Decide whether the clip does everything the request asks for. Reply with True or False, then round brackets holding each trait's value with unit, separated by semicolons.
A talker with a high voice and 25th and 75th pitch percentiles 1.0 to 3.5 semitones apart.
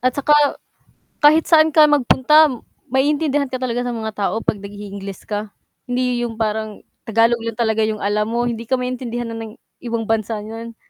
True (230 Hz; 2.8 semitones)